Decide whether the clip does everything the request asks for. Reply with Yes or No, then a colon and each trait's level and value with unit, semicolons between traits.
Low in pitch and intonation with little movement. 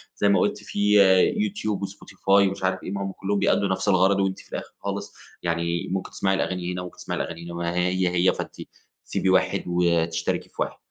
Yes: very low, 95 Hz; narrow, 2.1 semitones